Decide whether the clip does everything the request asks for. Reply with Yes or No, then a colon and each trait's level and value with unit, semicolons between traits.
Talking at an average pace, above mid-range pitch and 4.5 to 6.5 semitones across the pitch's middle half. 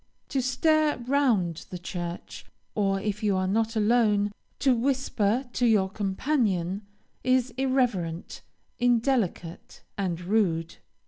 No: slow, 115 wpm; high, 215 Hz; average, 5.1 semitones